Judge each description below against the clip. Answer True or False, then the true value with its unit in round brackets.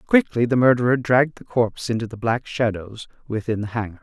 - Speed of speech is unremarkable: True (195 wpm)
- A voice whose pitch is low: True (115 Hz)